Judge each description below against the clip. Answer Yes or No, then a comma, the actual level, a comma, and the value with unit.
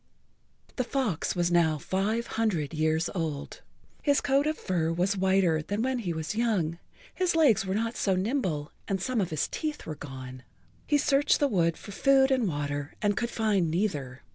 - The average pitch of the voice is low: No, high, 190 Hz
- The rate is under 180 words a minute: No, average, 185 wpm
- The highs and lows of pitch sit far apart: Yes, wide, 6.7 semitones